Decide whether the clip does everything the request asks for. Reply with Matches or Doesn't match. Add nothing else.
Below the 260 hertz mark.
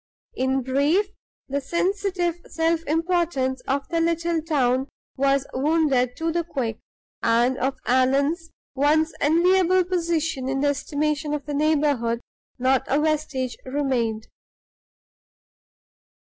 Doesn't match